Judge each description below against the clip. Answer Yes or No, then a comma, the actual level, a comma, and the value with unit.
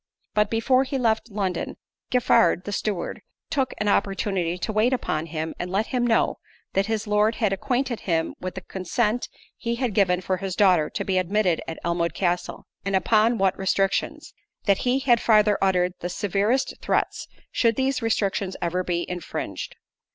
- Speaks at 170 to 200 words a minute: Yes, average, 175 wpm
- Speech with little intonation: No, average, 3.9 semitones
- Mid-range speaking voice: No, high, 200 Hz